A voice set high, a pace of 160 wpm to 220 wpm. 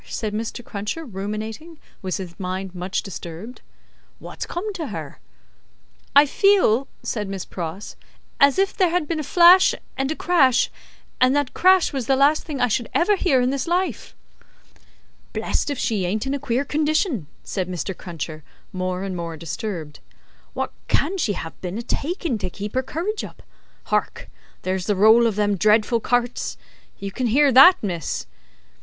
Yes: high, 235 Hz; average, 170 wpm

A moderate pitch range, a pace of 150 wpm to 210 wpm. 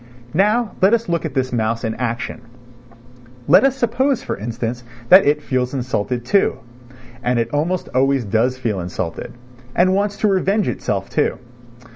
No: wide, 8.5 semitones; average, 160 wpm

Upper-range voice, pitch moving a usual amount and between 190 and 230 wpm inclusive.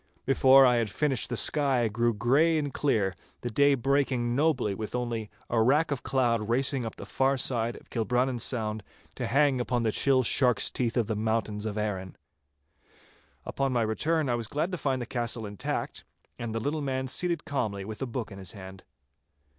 No: low, 120 Hz; average, 3.6 semitones; average, 195 wpm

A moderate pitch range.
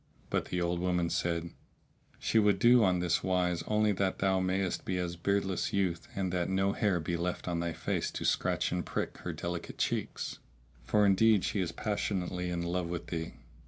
No: narrow, 2.2 semitones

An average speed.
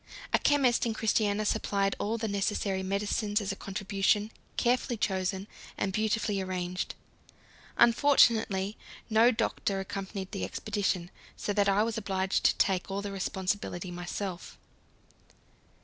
No: slow, 130 wpm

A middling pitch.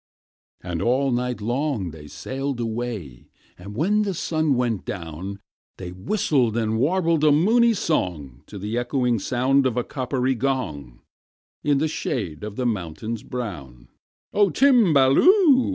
No: low, 125 Hz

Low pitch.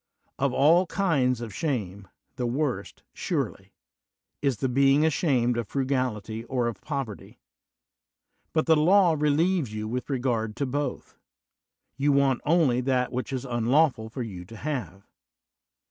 Yes: low, 130 Hz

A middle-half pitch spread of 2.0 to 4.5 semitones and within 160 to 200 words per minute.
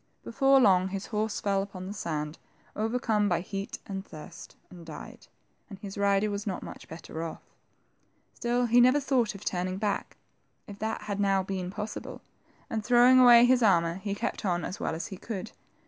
Yes: average, 3.2 semitones; average, 185 wpm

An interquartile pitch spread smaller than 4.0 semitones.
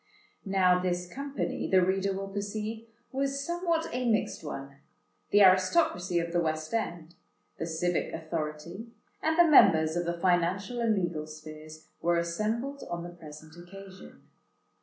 No: average, 4.6 semitones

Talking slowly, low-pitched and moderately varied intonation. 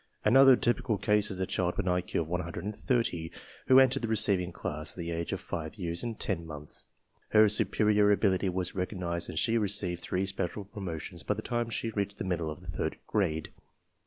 No: average, 200 wpm; very low, 95 Hz; average, 3.8 semitones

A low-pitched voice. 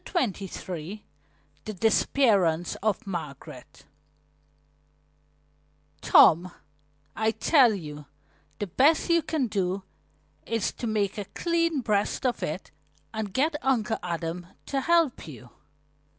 No: high, 210 Hz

